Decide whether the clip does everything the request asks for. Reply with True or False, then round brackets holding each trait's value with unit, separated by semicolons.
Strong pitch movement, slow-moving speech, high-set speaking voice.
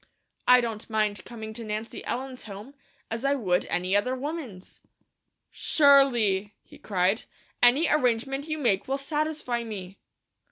False (4.9 semitones; 130 wpm; 235 Hz)